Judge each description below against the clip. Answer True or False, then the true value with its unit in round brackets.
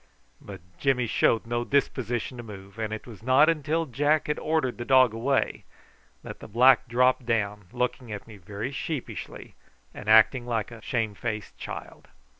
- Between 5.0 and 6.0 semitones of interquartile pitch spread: False (3.4 semitones)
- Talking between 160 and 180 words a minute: True (165 wpm)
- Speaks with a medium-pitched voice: False (120 Hz)